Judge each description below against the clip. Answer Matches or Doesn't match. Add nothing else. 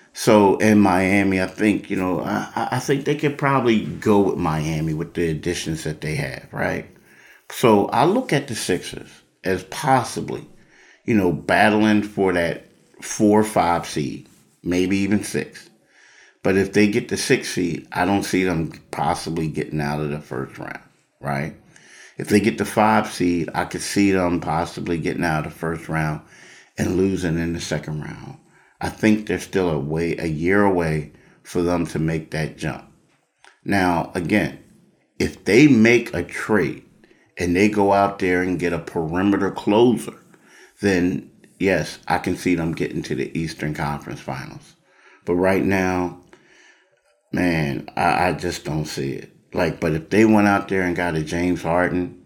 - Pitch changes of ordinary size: Matches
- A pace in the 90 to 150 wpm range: Doesn't match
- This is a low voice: Matches